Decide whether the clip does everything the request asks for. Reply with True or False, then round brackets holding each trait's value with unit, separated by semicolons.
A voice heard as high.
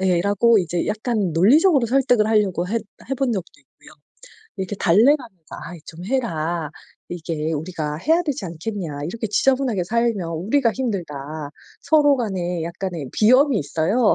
True (200 Hz)